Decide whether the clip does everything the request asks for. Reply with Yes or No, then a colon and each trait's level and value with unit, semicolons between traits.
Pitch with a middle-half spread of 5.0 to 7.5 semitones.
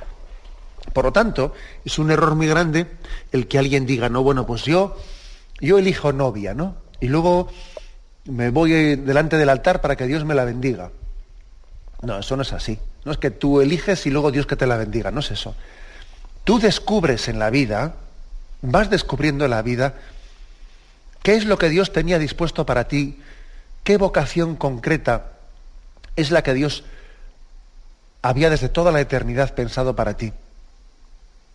Yes: wide, 5.5 semitones